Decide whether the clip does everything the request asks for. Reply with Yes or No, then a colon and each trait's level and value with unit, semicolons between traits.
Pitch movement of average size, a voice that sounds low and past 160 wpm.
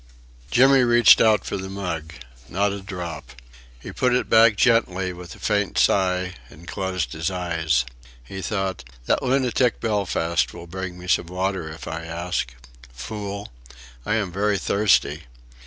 No: average, 3.4 semitones; very low, 95 Hz; average, 155 wpm